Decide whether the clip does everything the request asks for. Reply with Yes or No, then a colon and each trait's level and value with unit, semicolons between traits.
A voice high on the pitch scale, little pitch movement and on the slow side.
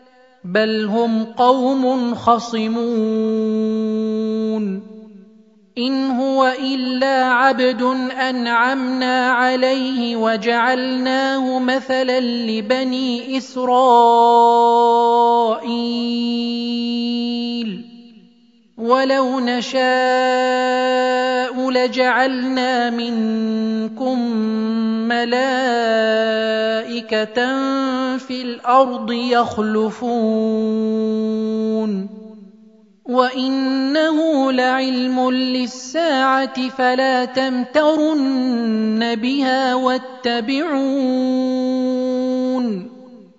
Yes: very high, 250 Hz; narrow, 2.3 semitones; slow, 40 wpm